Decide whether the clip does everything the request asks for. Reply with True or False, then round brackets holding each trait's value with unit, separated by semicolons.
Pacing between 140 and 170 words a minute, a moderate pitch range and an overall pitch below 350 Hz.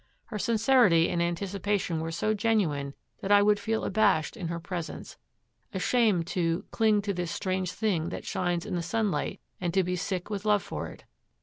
False (185 wpm; 3.6 semitones; 190 Hz)